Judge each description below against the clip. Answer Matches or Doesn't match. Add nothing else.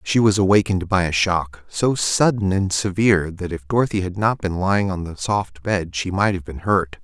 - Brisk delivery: Matches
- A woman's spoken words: Doesn't match